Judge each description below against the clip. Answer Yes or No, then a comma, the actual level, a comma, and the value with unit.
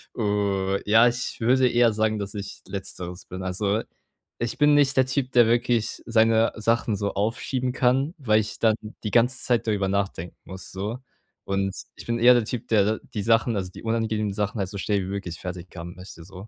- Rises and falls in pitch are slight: No, average, 3.3 semitones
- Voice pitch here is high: No, low, 110 Hz